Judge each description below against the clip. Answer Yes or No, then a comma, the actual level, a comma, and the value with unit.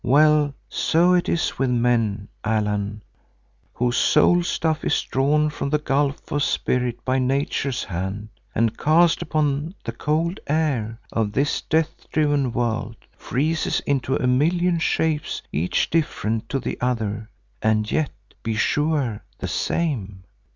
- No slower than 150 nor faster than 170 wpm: No, slow, 135 wpm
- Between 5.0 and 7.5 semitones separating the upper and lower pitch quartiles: Yes, average, 5.3 semitones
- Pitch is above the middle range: No, low, 135 Hz